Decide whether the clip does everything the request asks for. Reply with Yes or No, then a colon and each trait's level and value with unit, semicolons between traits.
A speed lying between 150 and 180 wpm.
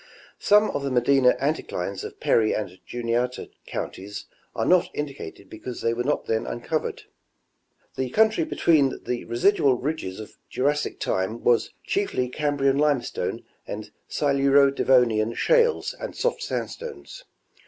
No: average, 140 wpm